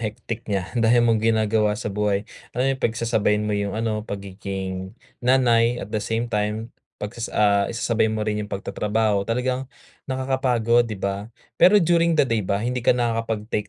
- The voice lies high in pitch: No, low, 110 Hz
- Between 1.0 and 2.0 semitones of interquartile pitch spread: No, narrow, 2.4 semitones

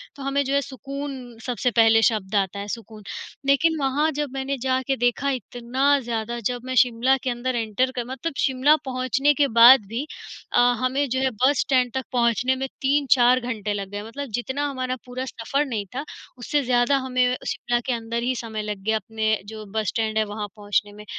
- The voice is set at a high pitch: Yes, very high, 250 Hz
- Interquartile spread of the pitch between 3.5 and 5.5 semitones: No, average, 3.1 semitones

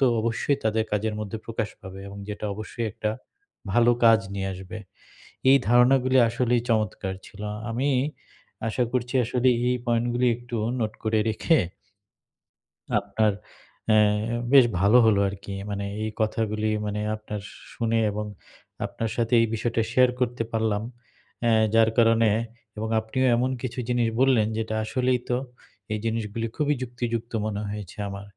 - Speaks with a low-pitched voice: Yes, low, 115 Hz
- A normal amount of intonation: No, narrow, 2.2 semitones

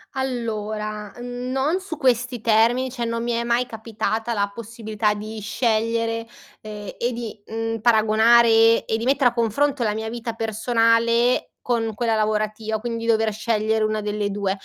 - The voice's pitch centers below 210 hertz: No, high, 225 Hz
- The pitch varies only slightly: Yes, narrow, 1.6 semitones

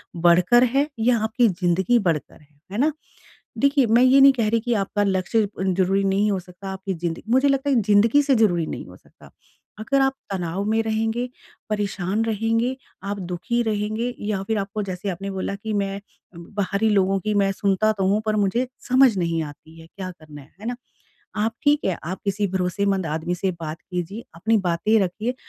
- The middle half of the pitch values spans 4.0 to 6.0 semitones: No, average, 3.5 semitones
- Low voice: No, high, 200 Hz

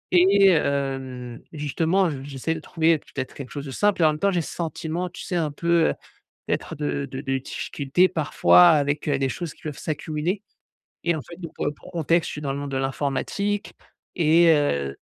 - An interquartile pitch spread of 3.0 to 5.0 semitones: Yes, average, 3.5 semitones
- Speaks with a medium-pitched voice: Yes, medium, 155 Hz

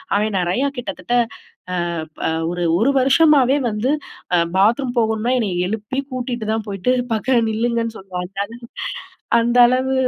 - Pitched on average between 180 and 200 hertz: No, high, 225 Hz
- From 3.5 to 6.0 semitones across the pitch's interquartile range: Yes, average, 3.9 semitones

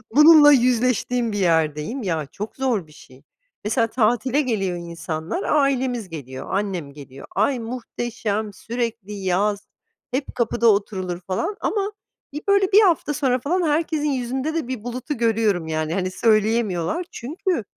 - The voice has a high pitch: Yes, high, 230 Hz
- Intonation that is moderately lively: No, wide, 6.1 semitones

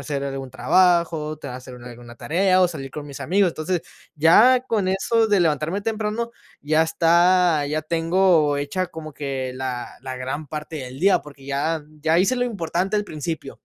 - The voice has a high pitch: No, medium, 160 Hz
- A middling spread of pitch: Yes, average, 4.6 semitones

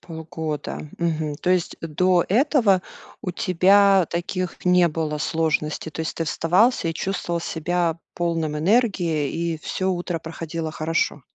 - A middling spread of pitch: No, narrow, 2.3 semitones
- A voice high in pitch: No, medium, 170 Hz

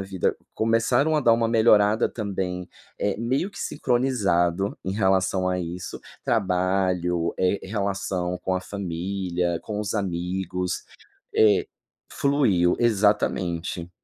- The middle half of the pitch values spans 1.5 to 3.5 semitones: Yes, average, 3.2 semitones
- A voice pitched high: No, very low, 95 Hz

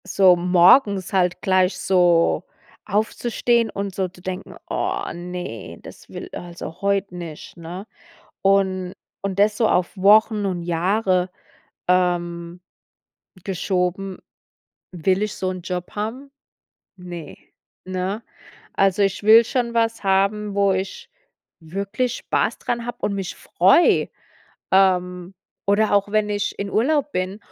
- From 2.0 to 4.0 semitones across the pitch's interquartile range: Yes, narrow, 2.4 semitones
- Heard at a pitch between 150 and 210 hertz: Yes, high, 190 Hz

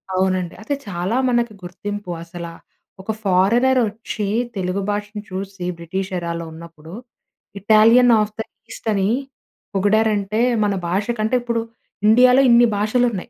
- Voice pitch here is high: Yes, high, 205 Hz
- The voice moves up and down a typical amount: Yes, average, 3.3 semitones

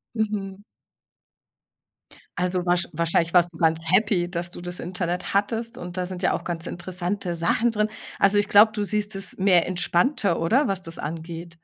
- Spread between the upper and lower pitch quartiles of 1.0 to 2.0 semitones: No, average, 2.8 semitones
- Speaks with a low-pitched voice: No, medium, 180 Hz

